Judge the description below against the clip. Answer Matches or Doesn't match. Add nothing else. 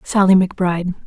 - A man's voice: Doesn't match